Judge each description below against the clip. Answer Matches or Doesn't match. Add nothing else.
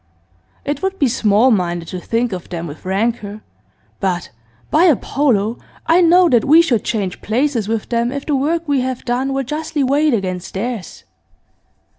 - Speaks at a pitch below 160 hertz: Doesn't match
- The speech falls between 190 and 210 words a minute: Doesn't match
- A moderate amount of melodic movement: Doesn't match